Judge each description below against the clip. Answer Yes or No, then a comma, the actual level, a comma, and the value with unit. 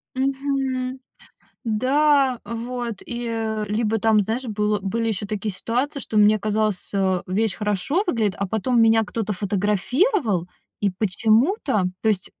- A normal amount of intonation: Yes, average, 3.4 semitones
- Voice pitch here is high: Yes, high, 220 Hz